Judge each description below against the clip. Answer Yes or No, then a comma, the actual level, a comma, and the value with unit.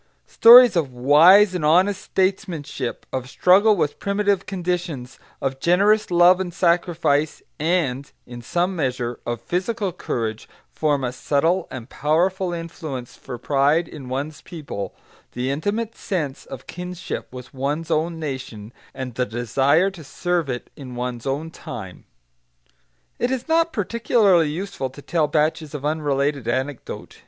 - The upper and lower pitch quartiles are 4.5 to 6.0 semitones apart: Yes, wide, 5.4 semitones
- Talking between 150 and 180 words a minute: No, average, 140 wpm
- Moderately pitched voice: Yes, medium, 155 Hz